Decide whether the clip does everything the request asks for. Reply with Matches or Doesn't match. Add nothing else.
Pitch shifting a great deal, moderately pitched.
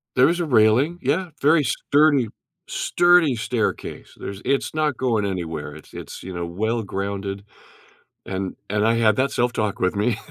Doesn't match